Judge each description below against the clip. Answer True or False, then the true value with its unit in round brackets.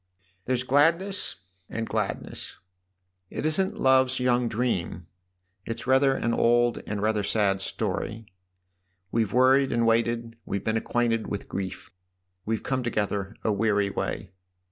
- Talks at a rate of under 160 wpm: True (140 wpm)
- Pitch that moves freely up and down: False (3.6 semitones)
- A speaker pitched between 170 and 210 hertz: False (115 Hz)